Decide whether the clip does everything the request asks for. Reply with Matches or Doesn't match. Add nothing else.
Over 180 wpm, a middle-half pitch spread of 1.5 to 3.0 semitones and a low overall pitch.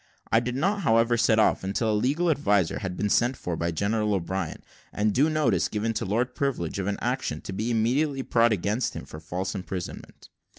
Doesn't match